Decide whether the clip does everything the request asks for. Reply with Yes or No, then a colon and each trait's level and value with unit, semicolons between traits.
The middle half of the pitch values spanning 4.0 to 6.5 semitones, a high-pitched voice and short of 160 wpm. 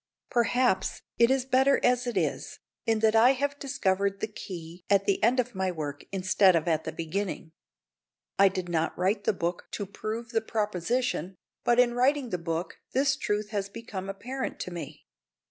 No: average, 4.9 semitones; high, 205 Hz; average, 180 wpm